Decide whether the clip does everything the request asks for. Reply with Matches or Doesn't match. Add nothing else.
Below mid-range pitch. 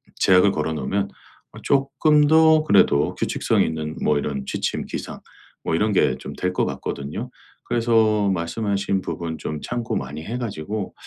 Matches